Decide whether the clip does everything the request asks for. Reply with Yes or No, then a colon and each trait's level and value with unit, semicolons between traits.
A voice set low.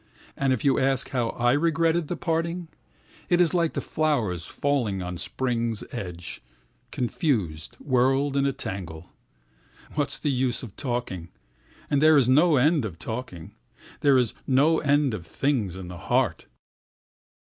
Yes: low, 130 Hz